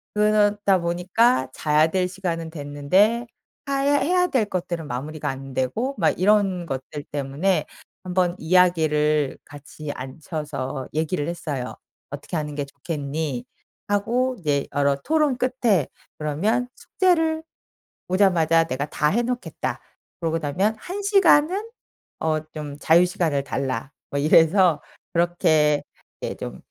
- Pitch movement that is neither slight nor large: No, wide, 6.1 semitones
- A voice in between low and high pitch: Yes, medium, 165 Hz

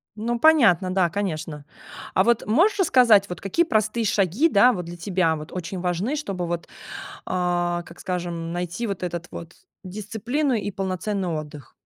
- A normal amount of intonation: Yes, average, 4.2 semitones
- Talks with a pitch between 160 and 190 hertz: Yes, medium, 185 Hz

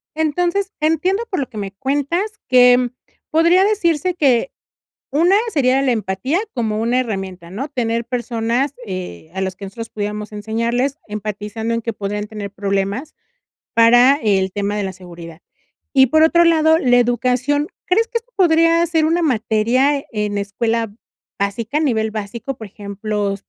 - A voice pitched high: Yes, high, 235 Hz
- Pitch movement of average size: No, wide, 6.4 semitones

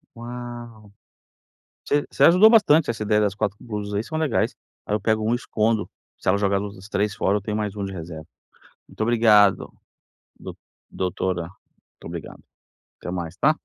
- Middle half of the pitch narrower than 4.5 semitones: Yes, average, 3.2 semitones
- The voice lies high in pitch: No, low, 105 Hz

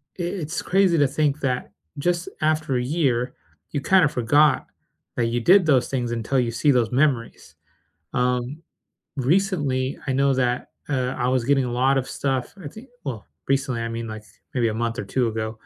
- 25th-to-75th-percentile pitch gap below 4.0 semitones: Yes, average, 3.4 semitones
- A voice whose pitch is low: Yes, low, 130 Hz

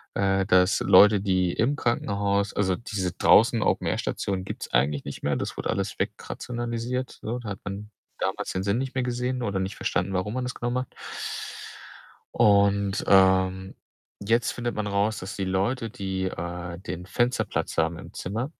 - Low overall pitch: Yes, low, 100 Hz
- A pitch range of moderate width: Yes, average, 3.8 semitones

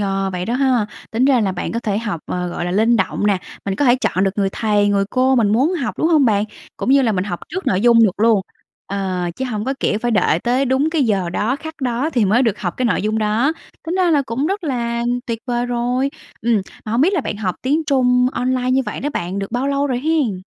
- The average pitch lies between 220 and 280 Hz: Yes, high, 235 Hz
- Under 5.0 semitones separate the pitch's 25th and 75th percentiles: Yes, average, 4.5 semitones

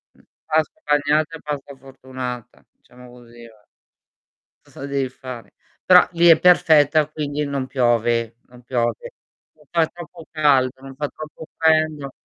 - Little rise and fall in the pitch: No, average, 3.9 semitones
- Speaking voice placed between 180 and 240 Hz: No, medium, 140 Hz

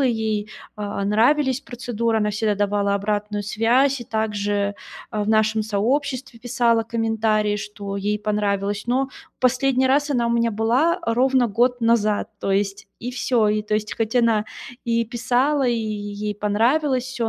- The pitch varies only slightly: No, average, 3.0 semitones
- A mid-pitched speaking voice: No, high, 225 Hz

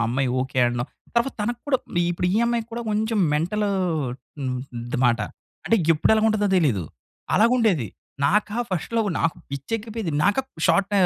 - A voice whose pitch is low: No, high, 200 Hz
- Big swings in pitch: Yes, wide, 8.0 semitones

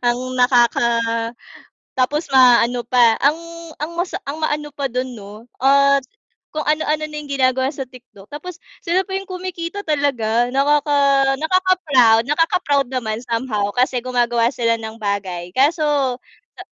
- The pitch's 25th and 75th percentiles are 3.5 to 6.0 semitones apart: Yes, average, 4.1 semitones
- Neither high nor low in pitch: No, very high, 265 Hz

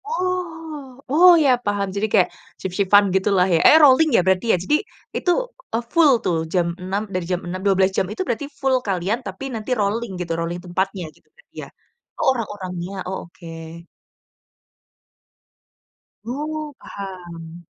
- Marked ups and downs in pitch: Yes, wide, 7.0 semitones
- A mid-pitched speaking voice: No, high, 200 Hz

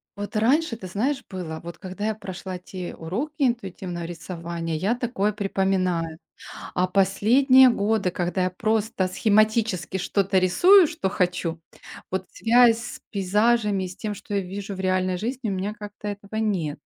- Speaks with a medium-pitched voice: No, high, 195 Hz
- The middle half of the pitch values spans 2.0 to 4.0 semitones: Yes, average, 3.3 semitones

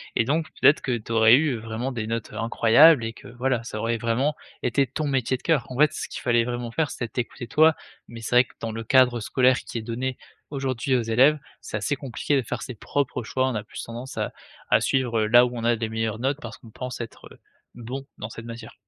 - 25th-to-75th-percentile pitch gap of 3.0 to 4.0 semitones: No, narrow, 2.5 semitones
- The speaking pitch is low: Yes, low, 120 Hz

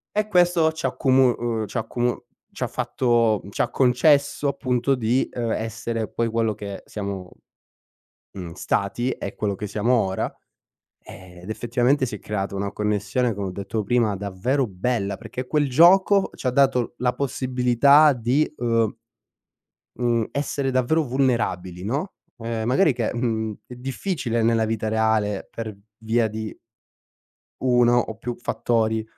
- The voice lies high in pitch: No, low, 120 Hz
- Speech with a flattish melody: No, average, 3.2 semitones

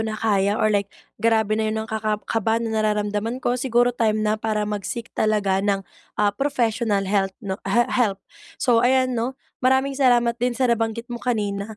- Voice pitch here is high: Yes, high, 220 Hz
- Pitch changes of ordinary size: No, narrow, 2.3 semitones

